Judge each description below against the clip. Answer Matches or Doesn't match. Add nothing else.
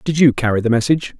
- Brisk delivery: Matches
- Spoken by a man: Matches